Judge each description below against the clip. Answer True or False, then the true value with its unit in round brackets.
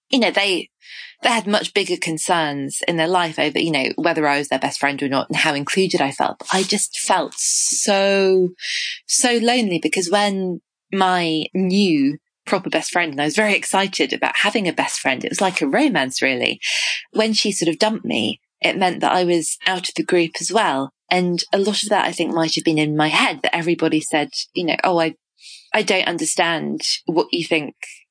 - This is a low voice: False (180 Hz)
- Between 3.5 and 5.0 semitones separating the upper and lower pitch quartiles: True (4.2 semitones)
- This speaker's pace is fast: True (215 wpm)